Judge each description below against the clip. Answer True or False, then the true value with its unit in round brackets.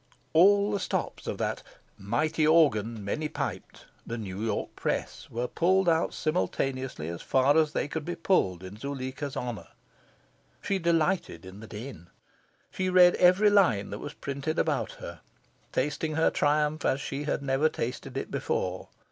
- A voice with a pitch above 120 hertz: True (140 Hz)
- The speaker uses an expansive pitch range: True (5.8 semitones)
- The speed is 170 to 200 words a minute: False (160 wpm)